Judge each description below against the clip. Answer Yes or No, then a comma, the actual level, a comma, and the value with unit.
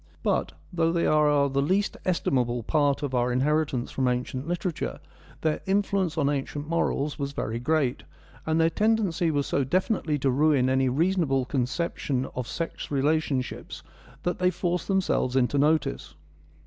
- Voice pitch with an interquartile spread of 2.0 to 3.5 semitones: No, average, 4.1 semitones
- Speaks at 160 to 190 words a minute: No, average, 150 wpm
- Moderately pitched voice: Yes, medium, 145 Hz